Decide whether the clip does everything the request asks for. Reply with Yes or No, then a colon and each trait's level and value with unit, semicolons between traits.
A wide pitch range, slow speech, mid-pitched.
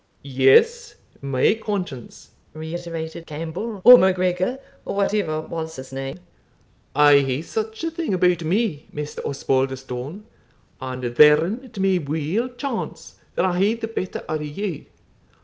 Yes: wide, 6.2 semitones; slow, 130 wpm; medium, 165 Hz